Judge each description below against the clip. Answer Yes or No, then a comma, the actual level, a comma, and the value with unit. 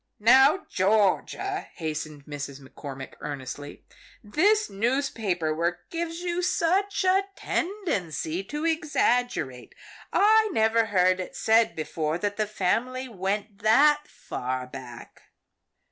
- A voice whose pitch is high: Yes, high, 215 Hz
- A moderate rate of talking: No, slow, 110 wpm